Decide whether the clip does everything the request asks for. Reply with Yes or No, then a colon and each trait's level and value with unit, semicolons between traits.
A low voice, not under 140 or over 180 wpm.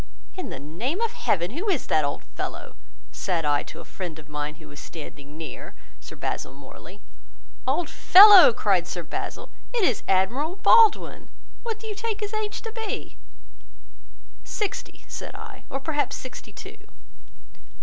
No: very high, 255 Hz; average, 160 wpm